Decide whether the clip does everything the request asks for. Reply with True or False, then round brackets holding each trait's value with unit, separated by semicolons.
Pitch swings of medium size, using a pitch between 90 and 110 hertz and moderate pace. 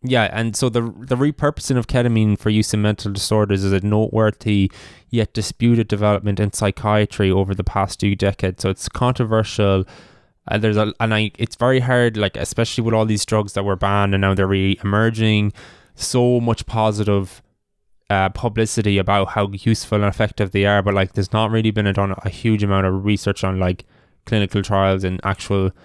False (2.2 semitones; 105 Hz; 190 wpm)